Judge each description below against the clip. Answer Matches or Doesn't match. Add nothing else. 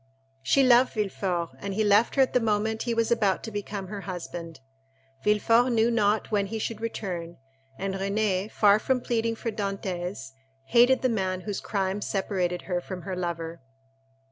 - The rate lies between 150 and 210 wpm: Matches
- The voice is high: Matches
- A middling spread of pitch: Matches